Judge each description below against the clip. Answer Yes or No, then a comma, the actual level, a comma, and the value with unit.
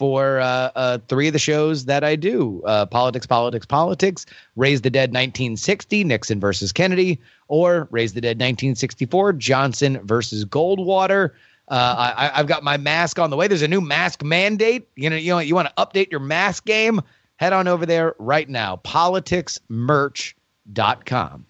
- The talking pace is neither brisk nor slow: Yes, average, 170 wpm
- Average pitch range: No, wide, 5.8 semitones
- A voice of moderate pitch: Yes, medium, 150 Hz